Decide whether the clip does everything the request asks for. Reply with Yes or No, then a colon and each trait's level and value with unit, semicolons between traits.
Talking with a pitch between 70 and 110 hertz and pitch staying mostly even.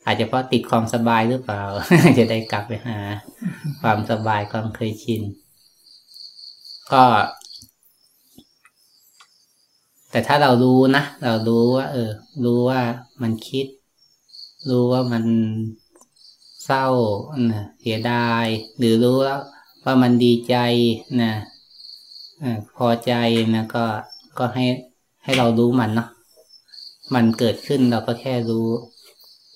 No: low, 120 Hz; narrow, 2.1 semitones